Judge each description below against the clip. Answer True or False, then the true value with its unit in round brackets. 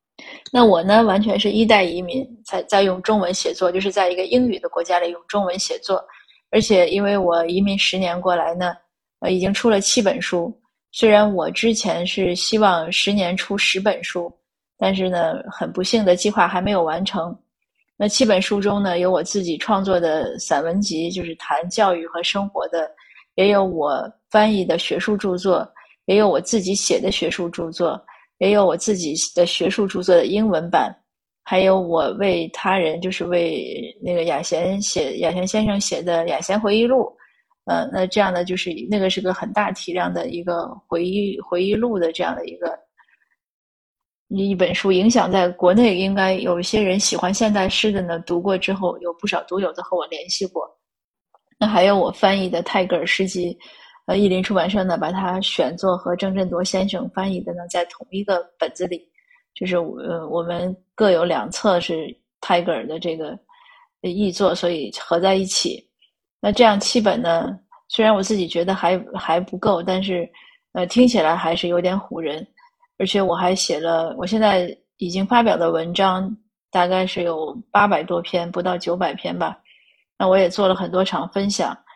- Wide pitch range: False (2.9 semitones)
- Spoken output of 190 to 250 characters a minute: False (265 characters per minute)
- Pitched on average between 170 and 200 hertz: True (185 Hz)